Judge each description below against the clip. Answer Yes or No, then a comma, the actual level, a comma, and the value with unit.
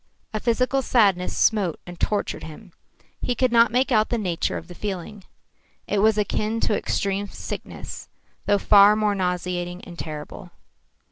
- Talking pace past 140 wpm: Yes, average, 155 wpm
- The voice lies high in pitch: Yes, high, 205 Hz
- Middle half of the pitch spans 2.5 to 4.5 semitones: Yes, average, 3.4 semitones